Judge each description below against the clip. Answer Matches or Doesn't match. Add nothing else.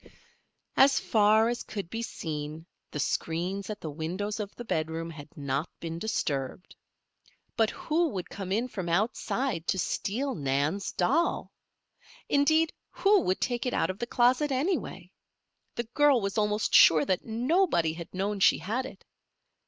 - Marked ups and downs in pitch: Matches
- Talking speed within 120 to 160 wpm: Matches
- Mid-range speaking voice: Doesn't match